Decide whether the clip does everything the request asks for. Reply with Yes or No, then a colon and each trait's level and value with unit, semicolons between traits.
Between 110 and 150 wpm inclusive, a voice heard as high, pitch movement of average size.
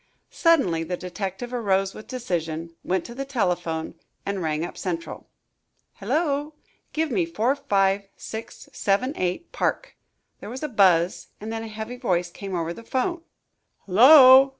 No: slow, 135 wpm; high, 200 Hz; wide, 6.3 semitones